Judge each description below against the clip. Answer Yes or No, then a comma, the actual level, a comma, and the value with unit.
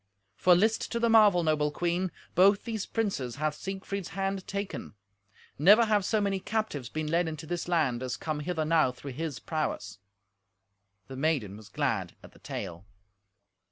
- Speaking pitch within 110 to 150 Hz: No, medium, 170 Hz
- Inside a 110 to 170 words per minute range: Yes, average, 165 wpm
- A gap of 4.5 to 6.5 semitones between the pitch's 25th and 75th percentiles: Yes, average, 4.9 semitones